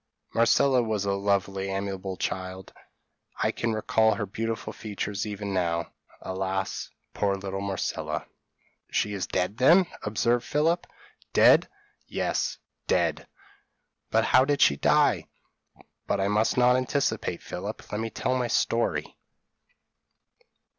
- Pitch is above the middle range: No, low, 105 Hz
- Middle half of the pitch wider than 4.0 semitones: No, average, 3.3 semitones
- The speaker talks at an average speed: No, slow, 125 wpm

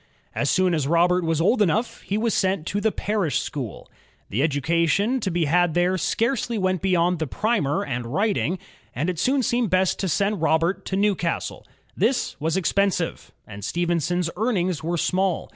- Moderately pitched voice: Yes, medium, 180 Hz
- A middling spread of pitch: Yes, average, 3.6 semitones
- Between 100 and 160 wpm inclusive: No, average, 175 wpm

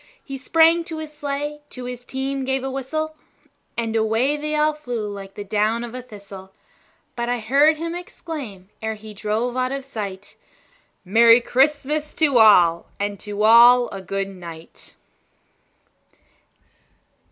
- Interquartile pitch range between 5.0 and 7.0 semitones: Yes, wide, 5.4 semitones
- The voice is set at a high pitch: Yes, high, 245 Hz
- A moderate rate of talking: Yes, average, 150 wpm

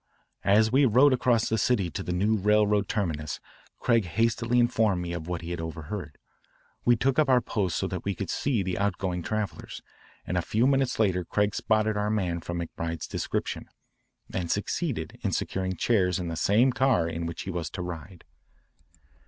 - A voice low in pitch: Yes, low, 100 Hz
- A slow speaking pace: No, average, 185 wpm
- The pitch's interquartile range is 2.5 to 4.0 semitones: No, average, 4.5 semitones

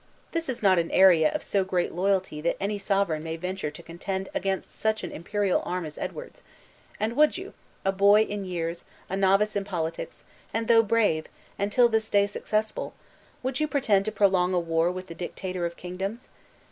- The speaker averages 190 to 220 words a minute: Yes, average, 195 wpm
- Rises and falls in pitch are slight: No, average, 3.3 semitones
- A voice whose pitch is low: No, high, 195 Hz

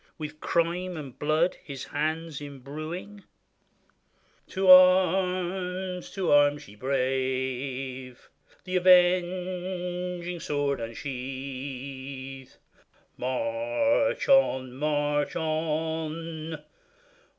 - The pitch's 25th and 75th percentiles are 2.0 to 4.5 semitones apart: No, average, 4.9 semitones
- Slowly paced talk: Yes, slow, 70 wpm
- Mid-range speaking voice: Yes, medium, 155 Hz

